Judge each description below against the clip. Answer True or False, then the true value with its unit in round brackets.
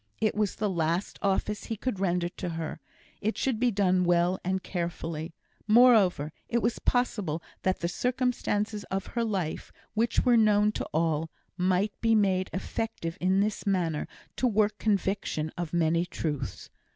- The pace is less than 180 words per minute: True (160 wpm)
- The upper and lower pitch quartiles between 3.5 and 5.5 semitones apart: True (3.9 semitones)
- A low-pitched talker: False (190 Hz)